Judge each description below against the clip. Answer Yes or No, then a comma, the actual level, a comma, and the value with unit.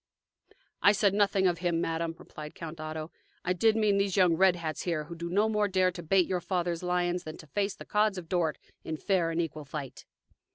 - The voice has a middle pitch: Yes, medium, 175 Hz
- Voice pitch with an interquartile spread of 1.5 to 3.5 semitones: Yes, average, 2.8 semitones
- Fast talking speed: Yes, fast, 220 wpm